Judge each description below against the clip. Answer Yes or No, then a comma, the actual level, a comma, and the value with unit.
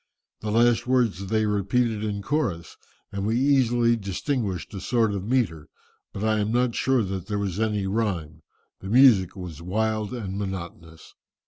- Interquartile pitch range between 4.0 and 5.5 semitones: No, average, 3.6 semitones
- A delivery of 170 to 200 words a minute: No, average, 160 wpm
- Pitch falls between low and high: No, low, 105 Hz